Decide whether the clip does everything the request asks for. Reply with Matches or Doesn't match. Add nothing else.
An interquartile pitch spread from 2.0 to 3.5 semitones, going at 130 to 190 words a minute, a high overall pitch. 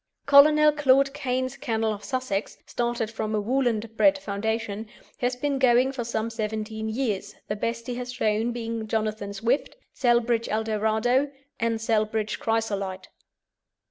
Matches